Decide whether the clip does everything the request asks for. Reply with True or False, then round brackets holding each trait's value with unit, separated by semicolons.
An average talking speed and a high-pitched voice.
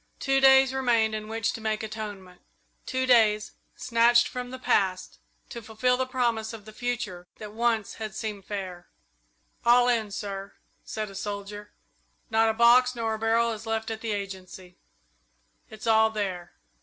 True (170 wpm; 220 Hz)